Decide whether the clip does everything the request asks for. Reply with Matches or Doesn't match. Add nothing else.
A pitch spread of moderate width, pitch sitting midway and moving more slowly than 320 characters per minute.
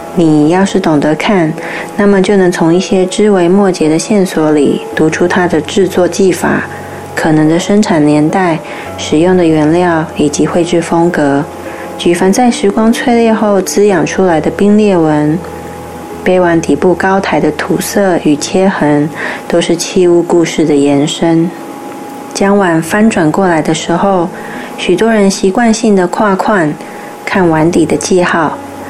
Matches